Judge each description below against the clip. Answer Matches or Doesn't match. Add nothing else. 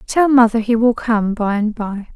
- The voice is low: Doesn't match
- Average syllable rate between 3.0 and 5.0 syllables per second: Matches